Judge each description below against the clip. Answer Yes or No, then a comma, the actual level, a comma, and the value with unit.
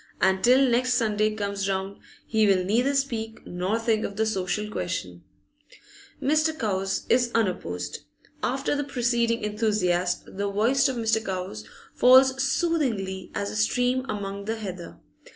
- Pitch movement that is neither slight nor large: Yes, average, 4.5 semitones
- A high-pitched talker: Yes, high, 215 Hz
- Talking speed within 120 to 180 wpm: Yes, average, 145 wpm